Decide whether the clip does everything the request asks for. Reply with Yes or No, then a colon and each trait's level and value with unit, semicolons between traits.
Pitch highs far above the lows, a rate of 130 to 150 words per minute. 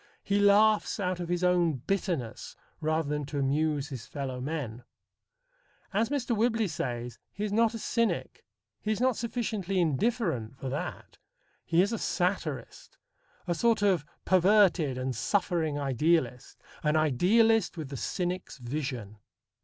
Yes: wide, 6.9 semitones; average, 145 wpm